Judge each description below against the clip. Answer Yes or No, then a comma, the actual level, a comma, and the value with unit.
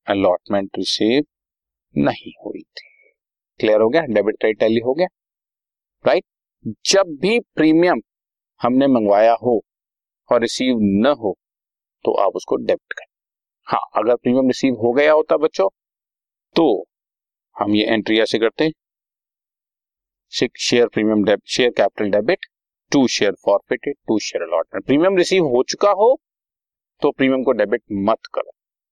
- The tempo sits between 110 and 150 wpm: Yes, average, 135 wpm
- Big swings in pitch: Yes, wide, 6.9 semitones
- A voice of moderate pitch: No, low, 130 Hz